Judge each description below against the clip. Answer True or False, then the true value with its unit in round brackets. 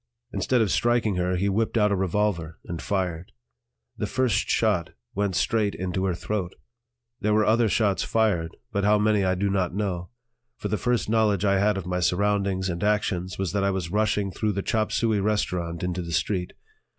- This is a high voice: False (100 Hz)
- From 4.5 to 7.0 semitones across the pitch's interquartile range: False (2.8 semitones)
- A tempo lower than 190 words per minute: False (195 wpm)